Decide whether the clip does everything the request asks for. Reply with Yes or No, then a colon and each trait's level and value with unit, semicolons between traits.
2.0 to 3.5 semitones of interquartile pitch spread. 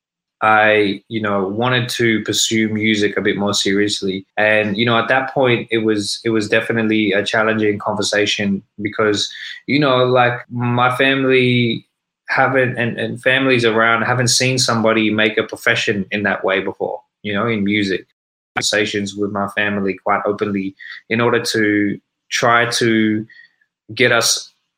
Yes: narrow, 2.5 semitones